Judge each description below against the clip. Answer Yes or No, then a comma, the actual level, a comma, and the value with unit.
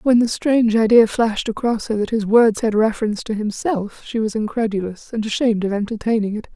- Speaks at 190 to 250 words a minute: Yes, average, 200 wpm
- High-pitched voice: Yes, high, 220 Hz